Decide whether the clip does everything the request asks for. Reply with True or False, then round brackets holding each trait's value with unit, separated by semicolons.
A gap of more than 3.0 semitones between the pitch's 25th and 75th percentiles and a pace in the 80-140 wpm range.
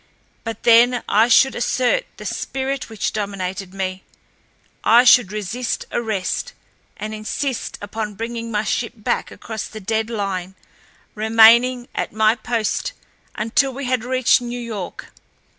False (2.6 semitones; 135 wpm)